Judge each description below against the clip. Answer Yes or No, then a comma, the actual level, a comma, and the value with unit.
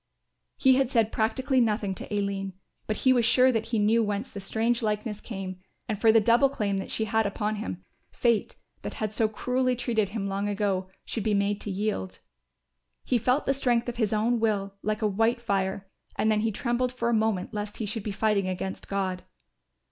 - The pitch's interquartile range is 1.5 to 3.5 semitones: Yes, average, 2.7 semitones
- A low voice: No, high, 215 Hz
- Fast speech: Yes, fast, 210 wpm